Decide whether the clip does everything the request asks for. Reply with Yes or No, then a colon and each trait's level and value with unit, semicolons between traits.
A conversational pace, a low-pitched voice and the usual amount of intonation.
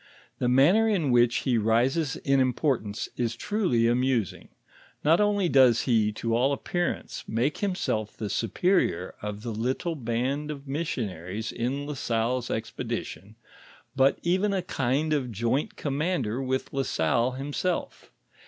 Yes: average, 145 wpm; low, 130 Hz; average, 4.6 semitones